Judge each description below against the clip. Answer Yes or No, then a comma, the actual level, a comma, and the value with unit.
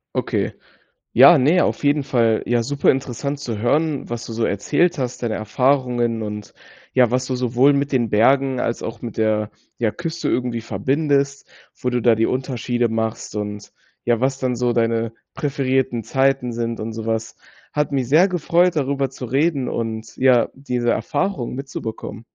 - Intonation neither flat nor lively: Yes, average, 3.3 semitones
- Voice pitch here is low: Yes, low, 125 Hz